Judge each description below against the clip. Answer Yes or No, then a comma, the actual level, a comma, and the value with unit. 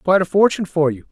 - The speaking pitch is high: No, medium, 175 Hz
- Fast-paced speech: Yes, fast, 270 wpm